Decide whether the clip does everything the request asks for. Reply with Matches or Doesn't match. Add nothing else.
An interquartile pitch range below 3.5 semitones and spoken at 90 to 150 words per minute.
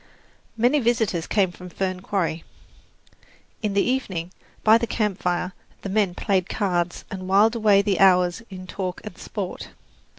Matches